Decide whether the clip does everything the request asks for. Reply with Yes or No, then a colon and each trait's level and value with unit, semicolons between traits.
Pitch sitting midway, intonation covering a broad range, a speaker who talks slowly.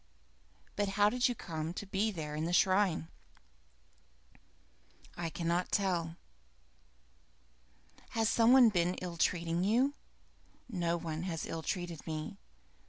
No: medium, 175 Hz; average, 3.8 semitones; slow, 125 wpm